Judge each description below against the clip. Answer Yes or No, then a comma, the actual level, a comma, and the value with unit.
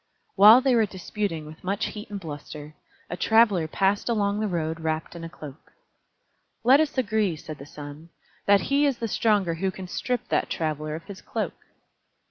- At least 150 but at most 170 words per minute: No, average, 185 wpm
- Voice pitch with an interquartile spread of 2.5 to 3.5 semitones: No, wide, 5.4 semitones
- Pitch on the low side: No, high, 190 Hz